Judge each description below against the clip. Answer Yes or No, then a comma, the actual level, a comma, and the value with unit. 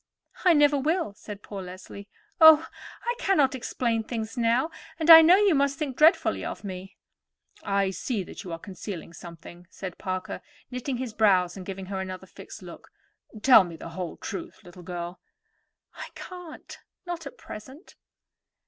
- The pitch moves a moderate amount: No, wide, 7.9 semitones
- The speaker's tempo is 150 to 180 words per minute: Yes, average, 160 wpm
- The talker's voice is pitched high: Yes, high, 220 Hz